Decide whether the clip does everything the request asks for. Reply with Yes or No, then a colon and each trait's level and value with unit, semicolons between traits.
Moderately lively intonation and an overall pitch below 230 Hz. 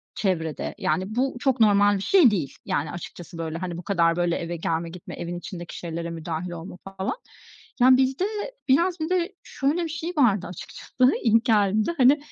No: wide, 7.4 semitones; high, 195 Hz